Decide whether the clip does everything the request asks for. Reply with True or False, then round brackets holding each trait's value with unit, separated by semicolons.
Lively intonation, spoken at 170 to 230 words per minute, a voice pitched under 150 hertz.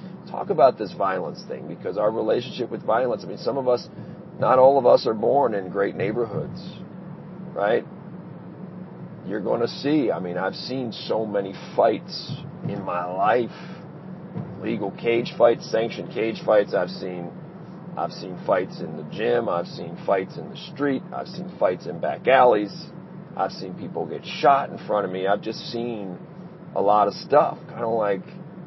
True (8.6 semitones; 175 wpm; 135 Hz)